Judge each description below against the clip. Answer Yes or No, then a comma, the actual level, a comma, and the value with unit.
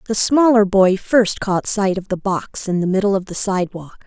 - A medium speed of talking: No, fast, 220 wpm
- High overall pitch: Yes, high, 195 Hz